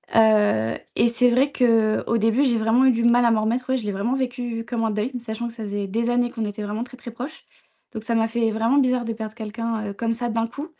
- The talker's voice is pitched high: Yes, high, 230 Hz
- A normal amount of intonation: No, narrow, 1.8 semitones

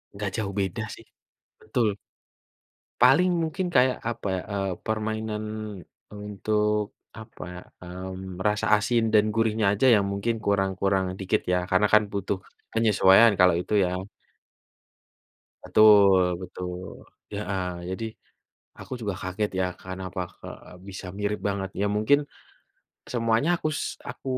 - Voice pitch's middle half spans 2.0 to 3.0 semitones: Yes, average, 2.7 semitones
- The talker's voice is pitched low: Yes, low, 105 Hz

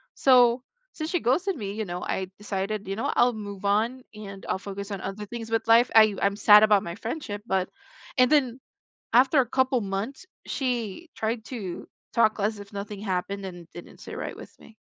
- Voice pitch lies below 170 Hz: No, high, 215 Hz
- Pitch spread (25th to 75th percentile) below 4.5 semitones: Yes, average, 3.5 semitones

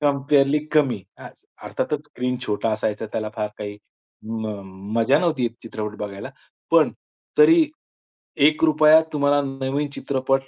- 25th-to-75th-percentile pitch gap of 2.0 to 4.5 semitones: No, average, 5.1 semitones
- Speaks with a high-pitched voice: No, low, 135 Hz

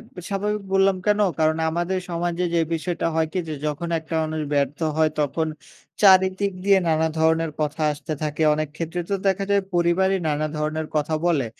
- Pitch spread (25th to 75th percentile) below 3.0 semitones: No, average, 3.3 semitones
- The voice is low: No, medium, 165 Hz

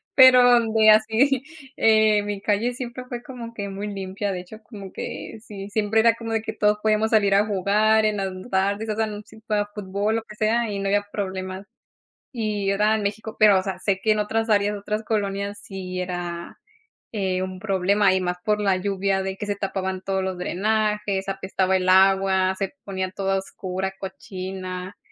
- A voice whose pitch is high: Yes, high, 200 Hz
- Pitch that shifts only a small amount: Yes, narrow, 2.2 semitones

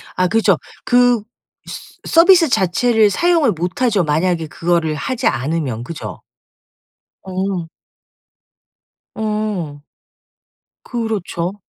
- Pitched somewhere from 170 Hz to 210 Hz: Yes, high, 190 Hz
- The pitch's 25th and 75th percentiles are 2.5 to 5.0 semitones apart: No, wide, 5.4 semitones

